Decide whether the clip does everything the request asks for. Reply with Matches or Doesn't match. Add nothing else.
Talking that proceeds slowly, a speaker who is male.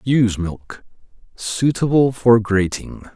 Matches